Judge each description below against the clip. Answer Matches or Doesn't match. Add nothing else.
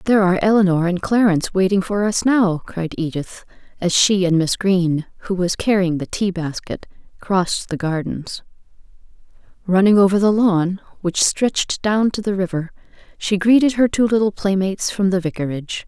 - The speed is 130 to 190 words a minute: Matches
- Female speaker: Matches